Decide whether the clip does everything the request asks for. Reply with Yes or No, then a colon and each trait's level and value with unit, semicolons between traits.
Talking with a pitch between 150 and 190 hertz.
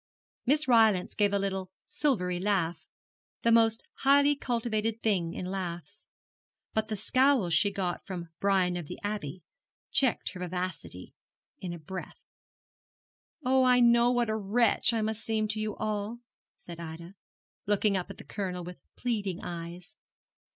No: high, 200 Hz